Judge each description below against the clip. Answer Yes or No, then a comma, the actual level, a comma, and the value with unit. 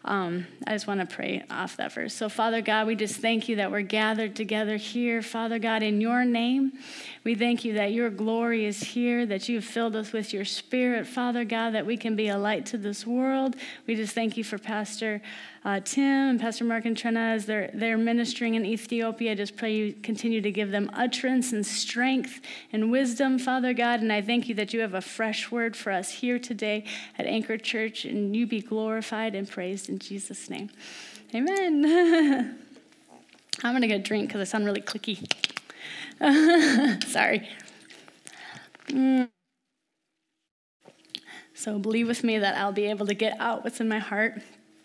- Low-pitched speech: No, high, 225 Hz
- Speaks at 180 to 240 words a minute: Yes, average, 190 wpm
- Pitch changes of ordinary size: No, narrow, 2.1 semitones